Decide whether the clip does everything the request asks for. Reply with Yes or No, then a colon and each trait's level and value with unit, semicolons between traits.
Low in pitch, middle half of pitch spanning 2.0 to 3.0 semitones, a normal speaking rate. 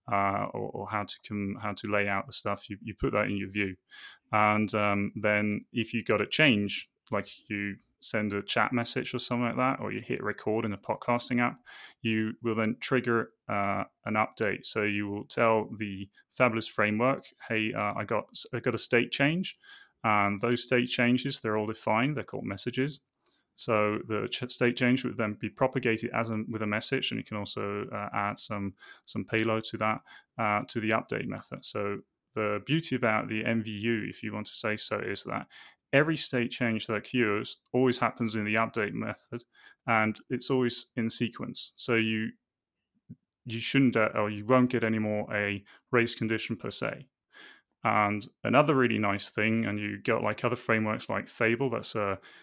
Yes: low, 110 Hz; narrow, 2.6 semitones; average, 195 wpm